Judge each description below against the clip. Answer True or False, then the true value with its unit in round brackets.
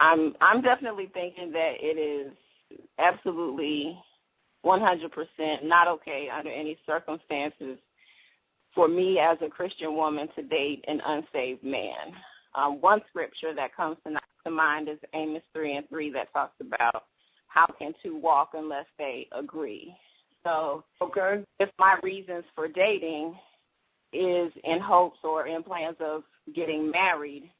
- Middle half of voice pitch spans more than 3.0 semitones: False (2.6 semitones)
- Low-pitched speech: False (160 Hz)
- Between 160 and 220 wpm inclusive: False (140 wpm)